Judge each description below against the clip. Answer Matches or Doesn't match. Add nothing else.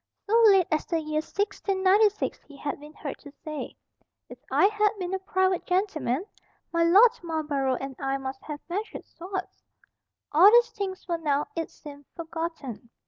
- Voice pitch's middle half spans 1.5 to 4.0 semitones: Doesn't match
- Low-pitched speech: Doesn't match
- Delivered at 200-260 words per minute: Doesn't match